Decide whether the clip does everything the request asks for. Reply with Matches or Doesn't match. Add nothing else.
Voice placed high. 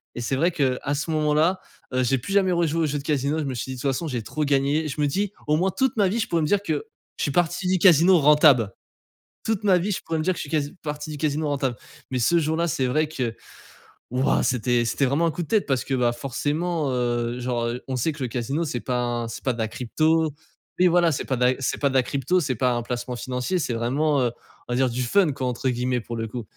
Doesn't match